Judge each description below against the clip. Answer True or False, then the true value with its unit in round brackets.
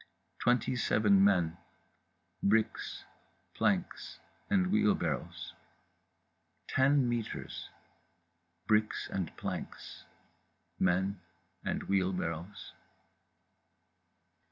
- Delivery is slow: True (60 wpm)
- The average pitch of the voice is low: True (100 Hz)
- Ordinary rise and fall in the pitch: True (5.0 semitones)